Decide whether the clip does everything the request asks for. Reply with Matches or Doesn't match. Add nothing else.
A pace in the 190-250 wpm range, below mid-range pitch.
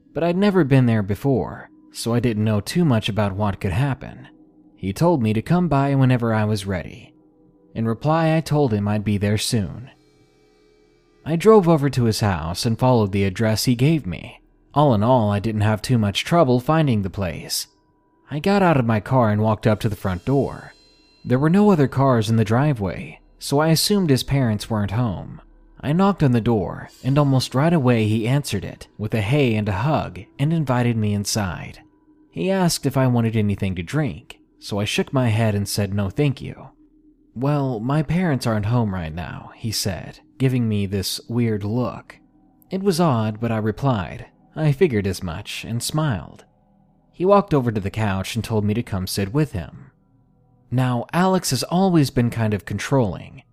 Matches